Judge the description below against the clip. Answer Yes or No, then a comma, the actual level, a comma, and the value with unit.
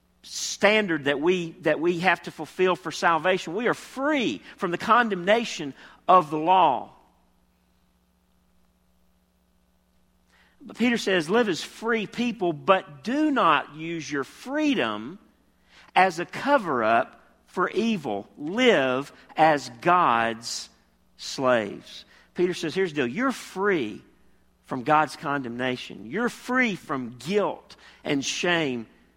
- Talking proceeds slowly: Yes, slow, 115 wpm